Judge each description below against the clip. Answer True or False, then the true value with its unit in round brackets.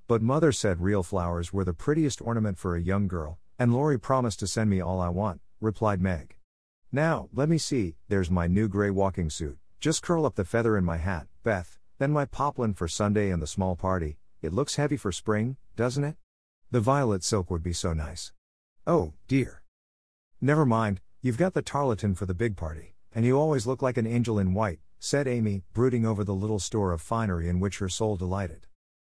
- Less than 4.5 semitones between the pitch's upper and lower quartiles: False (5.2 semitones)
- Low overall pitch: True (100 Hz)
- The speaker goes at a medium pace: False (210 wpm)